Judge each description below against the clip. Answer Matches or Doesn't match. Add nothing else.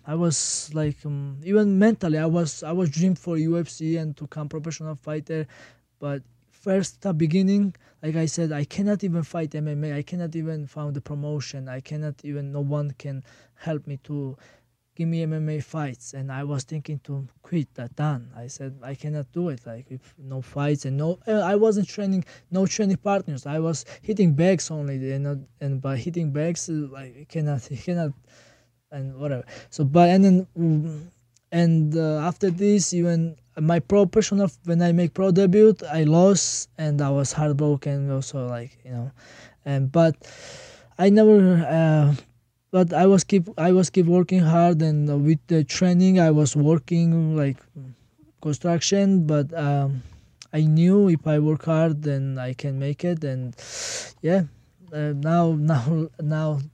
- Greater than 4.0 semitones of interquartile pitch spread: Doesn't match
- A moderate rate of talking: Matches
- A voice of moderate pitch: Matches